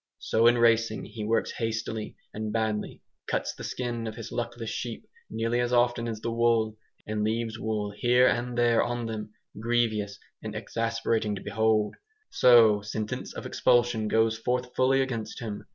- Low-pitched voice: Yes, low, 115 Hz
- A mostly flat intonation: Yes, narrow, 1.6 semitones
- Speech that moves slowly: No, average, 165 wpm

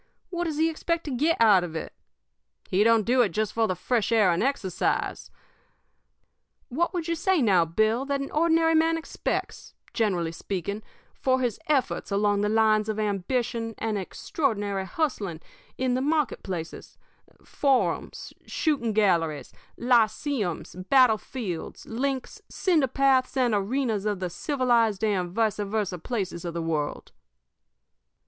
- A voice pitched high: Yes, high, 225 Hz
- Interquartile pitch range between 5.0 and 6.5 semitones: Yes, wide, 5.5 semitones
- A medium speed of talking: Yes, average, 145 wpm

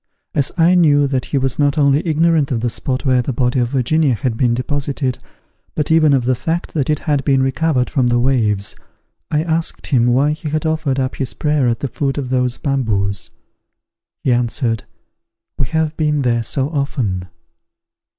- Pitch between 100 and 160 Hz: Yes, low, 135 Hz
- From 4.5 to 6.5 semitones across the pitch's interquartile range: No, average, 3.5 semitones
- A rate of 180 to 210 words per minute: Yes, average, 190 wpm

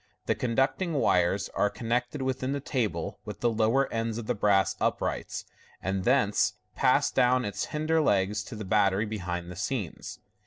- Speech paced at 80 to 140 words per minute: No, average, 165 wpm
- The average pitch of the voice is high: No, low, 115 Hz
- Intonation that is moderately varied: Yes, average, 4.6 semitones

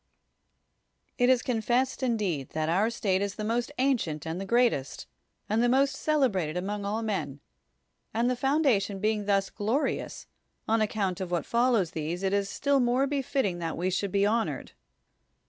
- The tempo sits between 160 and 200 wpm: Yes, average, 165 wpm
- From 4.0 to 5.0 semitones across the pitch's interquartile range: Yes, average, 4.6 semitones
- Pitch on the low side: No, high, 215 Hz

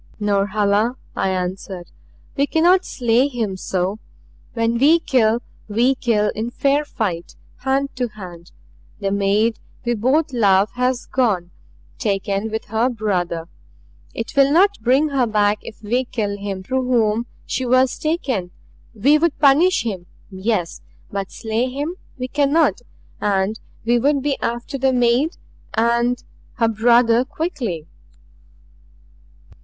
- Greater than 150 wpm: No, slow, 135 wpm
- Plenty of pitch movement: No, average, 4.5 semitones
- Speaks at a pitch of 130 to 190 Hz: No, high, 235 Hz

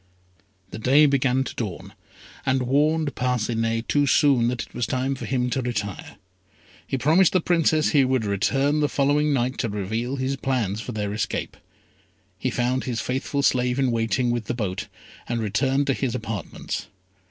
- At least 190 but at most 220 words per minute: No, average, 175 wpm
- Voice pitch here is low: Yes, low, 125 Hz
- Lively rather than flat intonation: No, average, 3.2 semitones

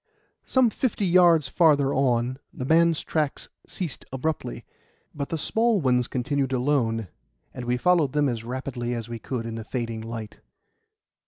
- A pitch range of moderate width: Yes, average, 4.9 semitones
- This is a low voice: Yes, low, 130 Hz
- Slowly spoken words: No, average, 155 wpm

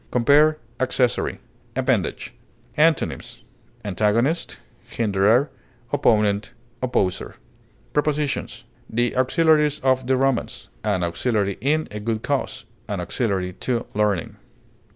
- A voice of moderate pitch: No, low, 120 Hz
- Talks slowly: Yes, slow, 95 wpm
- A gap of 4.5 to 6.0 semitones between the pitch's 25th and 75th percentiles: Yes, average, 5.1 semitones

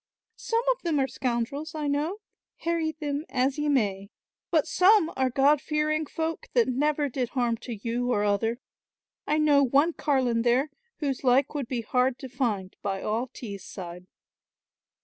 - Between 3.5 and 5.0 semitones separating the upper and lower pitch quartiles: Yes, average, 4.2 semitones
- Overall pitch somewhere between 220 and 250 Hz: No, very high, 270 Hz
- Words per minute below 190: Yes, average, 170 wpm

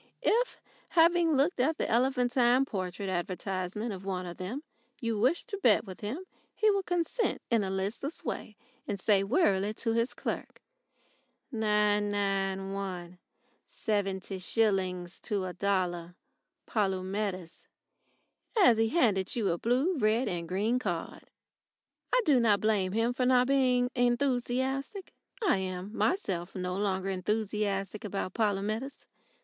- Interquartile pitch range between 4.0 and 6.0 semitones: Yes, average, 4.7 semitones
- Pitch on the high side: Yes, high, 210 Hz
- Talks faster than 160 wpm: No, slow, 135 wpm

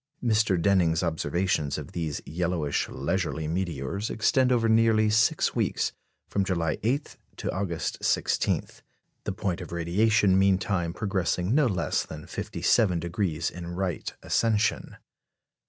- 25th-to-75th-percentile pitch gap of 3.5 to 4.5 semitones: Yes, average, 4.2 semitones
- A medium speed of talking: No, slow, 120 wpm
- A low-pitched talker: Yes, very low, 95 Hz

